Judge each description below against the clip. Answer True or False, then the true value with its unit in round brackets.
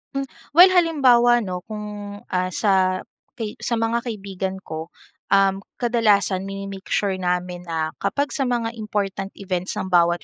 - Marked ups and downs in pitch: False (3.8 semitones)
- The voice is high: True (200 Hz)